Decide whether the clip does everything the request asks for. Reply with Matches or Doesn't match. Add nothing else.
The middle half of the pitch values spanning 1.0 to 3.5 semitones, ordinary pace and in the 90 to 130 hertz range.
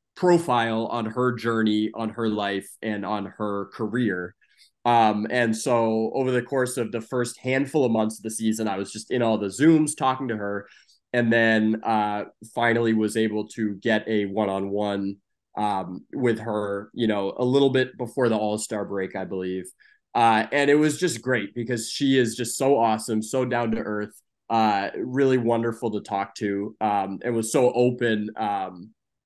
Matches